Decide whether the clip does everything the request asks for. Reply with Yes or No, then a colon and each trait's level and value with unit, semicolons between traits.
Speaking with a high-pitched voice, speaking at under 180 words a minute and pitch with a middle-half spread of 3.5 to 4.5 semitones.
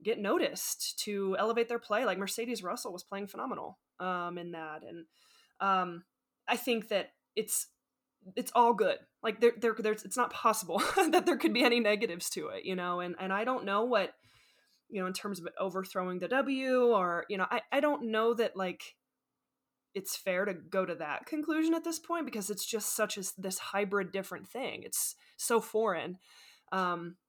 No: high, 210 Hz; average, 190 wpm; average, 4.2 semitones